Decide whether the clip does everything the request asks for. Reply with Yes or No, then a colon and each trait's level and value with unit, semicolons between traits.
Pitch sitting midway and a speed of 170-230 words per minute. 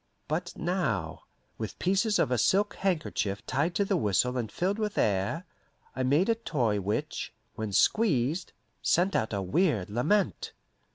No: medium, 145 Hz; average, 155 wpm